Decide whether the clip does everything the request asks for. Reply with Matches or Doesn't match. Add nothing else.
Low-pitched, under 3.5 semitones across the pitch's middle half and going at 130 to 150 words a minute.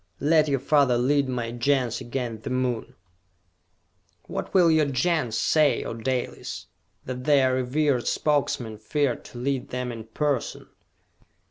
Matches